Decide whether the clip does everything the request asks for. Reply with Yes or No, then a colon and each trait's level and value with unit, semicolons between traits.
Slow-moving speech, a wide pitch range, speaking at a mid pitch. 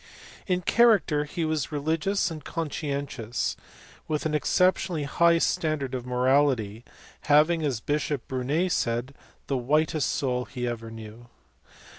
No: slow, 125 wpm; average, 4.2 semitones; medium, 145 Hz